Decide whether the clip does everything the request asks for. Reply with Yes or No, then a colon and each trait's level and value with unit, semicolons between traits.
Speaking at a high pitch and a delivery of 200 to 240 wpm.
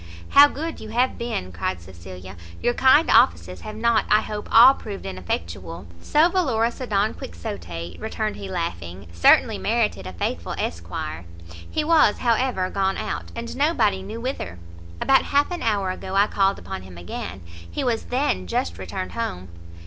No: high, 195 Hz; average, 165 wpm